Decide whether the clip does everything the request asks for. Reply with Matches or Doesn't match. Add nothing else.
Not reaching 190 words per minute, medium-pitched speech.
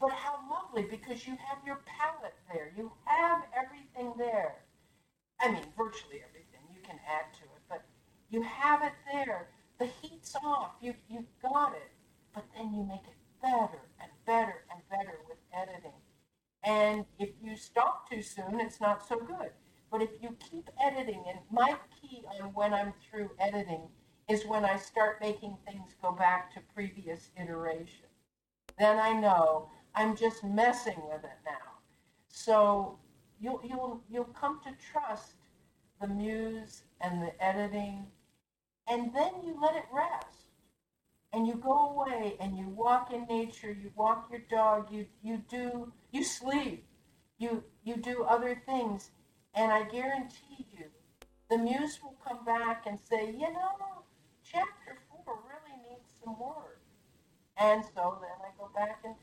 Doesn't match